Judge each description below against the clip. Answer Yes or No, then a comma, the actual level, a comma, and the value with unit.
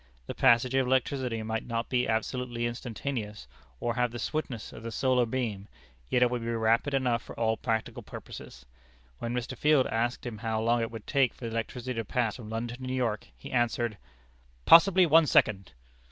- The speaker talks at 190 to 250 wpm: Yes, average, 195 wpm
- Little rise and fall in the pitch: Yes, narrow, 2.2 semitones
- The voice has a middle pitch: No, low, 120 Hz